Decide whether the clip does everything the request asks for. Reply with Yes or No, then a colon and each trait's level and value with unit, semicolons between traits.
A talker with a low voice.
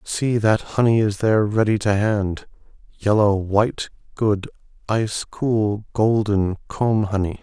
Yes: low, 105 Hz